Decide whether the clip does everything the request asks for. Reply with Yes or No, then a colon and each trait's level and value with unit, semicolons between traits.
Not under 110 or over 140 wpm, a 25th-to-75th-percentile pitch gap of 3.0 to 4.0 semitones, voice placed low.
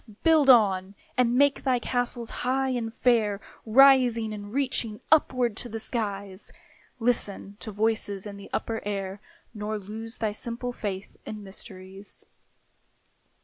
No: slow, 135 wpm; average, 3.3 semitones; high, 225 Hz